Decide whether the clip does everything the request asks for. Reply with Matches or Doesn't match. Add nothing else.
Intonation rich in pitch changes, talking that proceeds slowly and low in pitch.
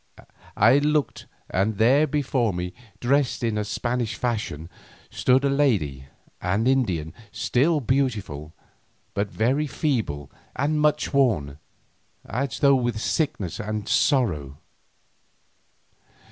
Matches